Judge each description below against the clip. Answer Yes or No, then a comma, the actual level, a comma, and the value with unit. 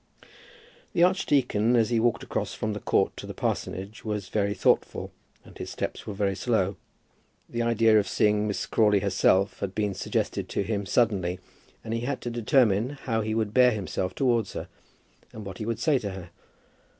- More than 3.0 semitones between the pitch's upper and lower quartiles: No, average, 2.7 semitones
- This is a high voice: No, low, 110 Hz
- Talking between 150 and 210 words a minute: Yes, average, 185 wpm